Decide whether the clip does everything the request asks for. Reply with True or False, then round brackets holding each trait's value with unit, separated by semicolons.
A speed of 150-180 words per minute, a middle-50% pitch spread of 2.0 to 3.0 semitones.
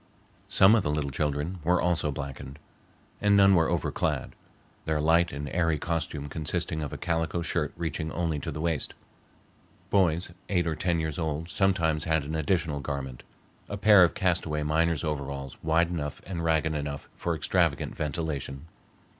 True (165 wpm; 2.6 semitones)